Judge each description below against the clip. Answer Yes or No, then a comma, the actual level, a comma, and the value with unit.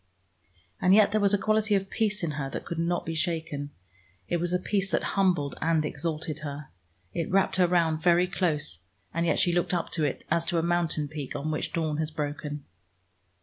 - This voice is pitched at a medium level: Yes, medium, 170 Hz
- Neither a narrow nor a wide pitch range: Yes, average, 3.0 semitones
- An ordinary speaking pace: No, fast, 210 wpm